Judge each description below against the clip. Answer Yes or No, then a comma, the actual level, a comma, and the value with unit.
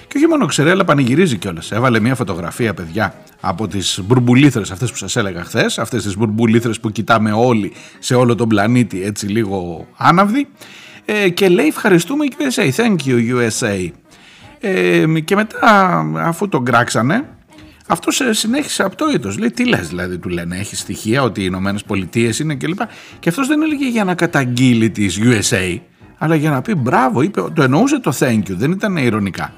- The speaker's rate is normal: No, fast, 175 wpm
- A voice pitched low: Yes, low, 120 Hz